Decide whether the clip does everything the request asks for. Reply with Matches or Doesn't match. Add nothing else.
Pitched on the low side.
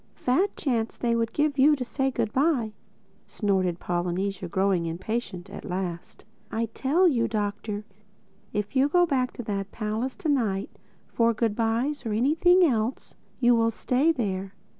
Doesn't match